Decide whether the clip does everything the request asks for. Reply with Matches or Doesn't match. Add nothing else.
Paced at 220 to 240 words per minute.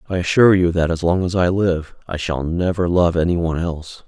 Matches